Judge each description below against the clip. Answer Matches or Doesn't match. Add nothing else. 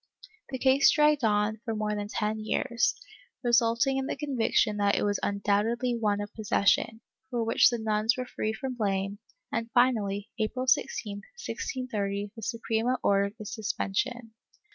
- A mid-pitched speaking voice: Doesn't match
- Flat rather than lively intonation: Doesn't match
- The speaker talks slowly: Doesn't match